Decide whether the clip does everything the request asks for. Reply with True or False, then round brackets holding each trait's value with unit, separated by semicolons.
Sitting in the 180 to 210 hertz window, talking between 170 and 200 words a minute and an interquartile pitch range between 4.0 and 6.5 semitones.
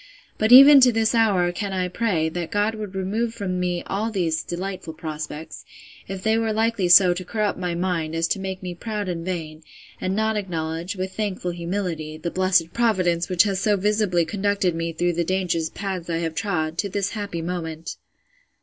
False (185 Hz; 195 wpm; 3.3 semitones)